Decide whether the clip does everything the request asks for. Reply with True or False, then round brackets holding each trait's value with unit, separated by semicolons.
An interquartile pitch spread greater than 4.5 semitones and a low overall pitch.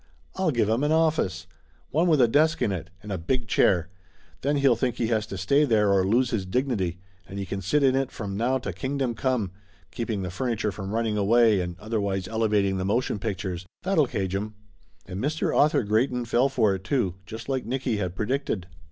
True (5.2 semitones; 110 Hz)